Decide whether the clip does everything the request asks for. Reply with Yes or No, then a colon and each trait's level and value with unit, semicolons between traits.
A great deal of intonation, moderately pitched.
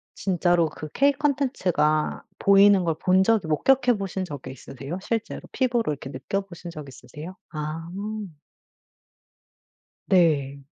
No: average, 4.8 semitones; medium, 175 Hz